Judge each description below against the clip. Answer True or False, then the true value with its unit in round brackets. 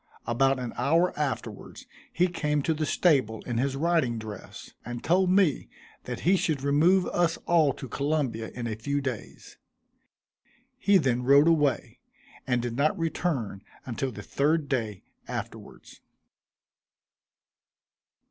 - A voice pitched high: False (140 Hz)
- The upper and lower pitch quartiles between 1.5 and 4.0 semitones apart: False (5.1 semitones)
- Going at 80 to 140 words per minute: True (135 wpm)